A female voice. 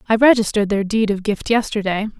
Yes: female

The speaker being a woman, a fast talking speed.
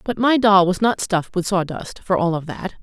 Yes: female; fast, 255 wpm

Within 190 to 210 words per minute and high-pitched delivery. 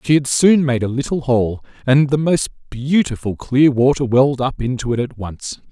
No: average, 200 wpm; low, 130 Hz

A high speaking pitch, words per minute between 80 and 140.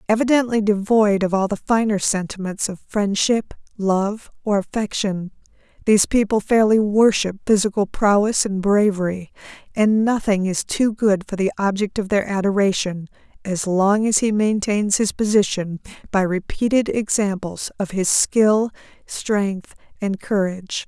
Yes: high, 205 Hz; slow, 135 wpm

